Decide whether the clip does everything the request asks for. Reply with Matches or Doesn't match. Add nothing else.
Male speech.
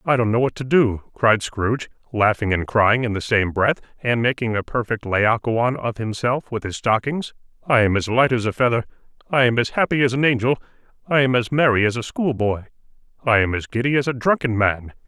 Matches